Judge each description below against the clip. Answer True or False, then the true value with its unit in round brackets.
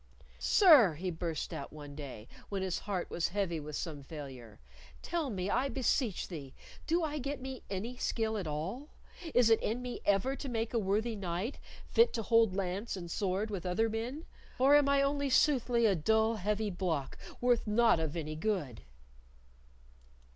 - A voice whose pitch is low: False (210 Hz)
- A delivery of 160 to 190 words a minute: True (180 wpm)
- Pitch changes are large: True (6.2 semitones)